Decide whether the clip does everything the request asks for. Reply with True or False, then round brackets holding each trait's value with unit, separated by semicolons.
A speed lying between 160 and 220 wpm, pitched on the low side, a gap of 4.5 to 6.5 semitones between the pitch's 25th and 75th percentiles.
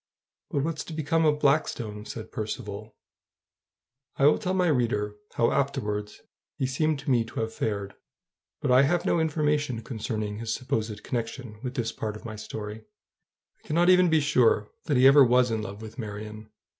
True (180 wpm; 120 Hz; 5.4 semitones)